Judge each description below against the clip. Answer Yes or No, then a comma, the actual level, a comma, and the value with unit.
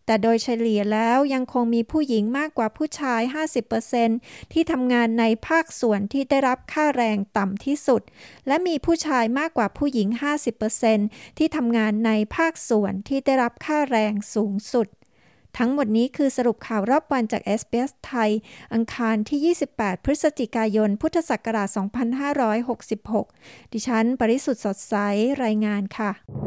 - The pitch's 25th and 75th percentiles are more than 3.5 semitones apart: Yes, average, 4.0 semitones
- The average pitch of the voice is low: No, high, 235 Hz